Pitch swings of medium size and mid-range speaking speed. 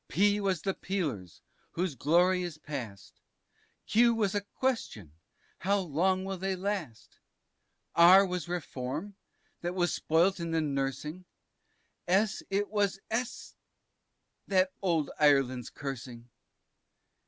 No: average, 4.9 semitones; slow, 120 wpm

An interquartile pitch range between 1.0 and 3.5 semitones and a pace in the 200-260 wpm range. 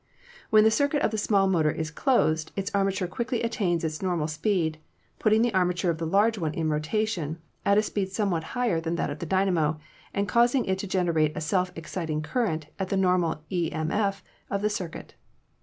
No: average, 4.4 semitones; fast, 205 wpm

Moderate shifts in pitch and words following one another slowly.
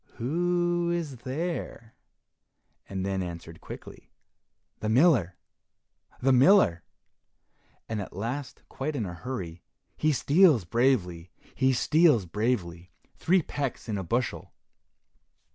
No: wide, 8.2 semitones; slow, 110 wpm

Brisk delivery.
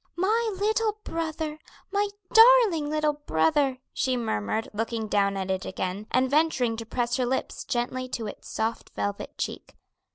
No: average, 155 wpm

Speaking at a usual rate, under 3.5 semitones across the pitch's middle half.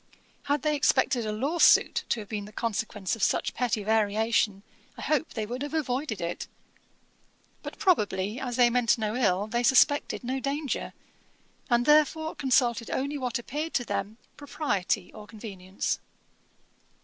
No: average, 150 wpm; average, 4.8 semitones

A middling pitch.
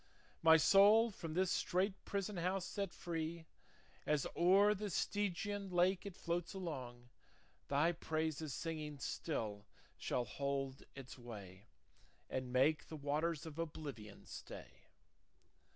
Yes: medium, 160 Hz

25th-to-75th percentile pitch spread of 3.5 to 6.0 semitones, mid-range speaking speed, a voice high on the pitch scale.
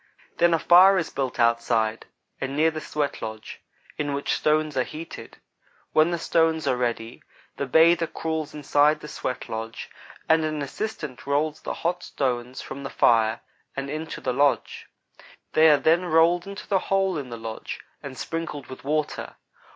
No: average, 4.1 semitones; average, 165 wpm; medium, 150 Hz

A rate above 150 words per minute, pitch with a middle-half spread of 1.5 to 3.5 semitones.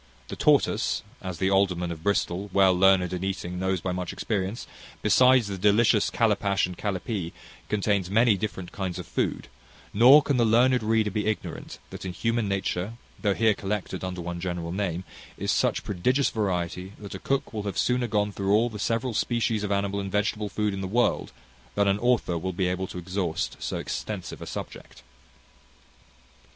Yes: average, 185 wpm; average, 2.8 semitones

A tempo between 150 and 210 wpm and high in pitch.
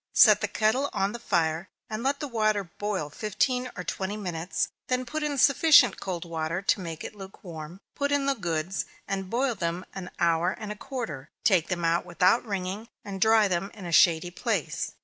Yes: average, 195 wpm; high, 195 Hz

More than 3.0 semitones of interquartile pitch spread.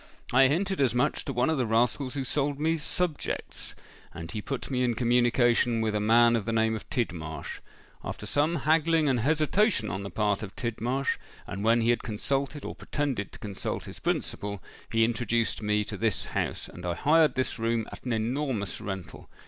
Yes: average, 4.4 semitones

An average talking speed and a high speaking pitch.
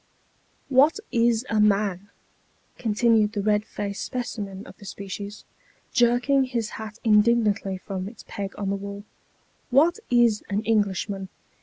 Yes: average, 150 wpm; high, 210 Hz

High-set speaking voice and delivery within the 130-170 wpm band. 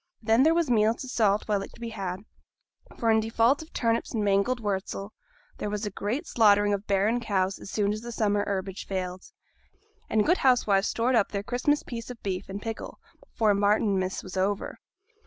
No: high, 210 Hz; average, 195 wpm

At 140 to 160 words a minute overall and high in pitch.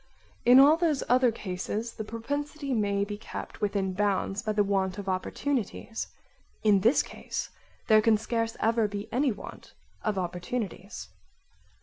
Yes: average, 150 wpm; high, 215 Hz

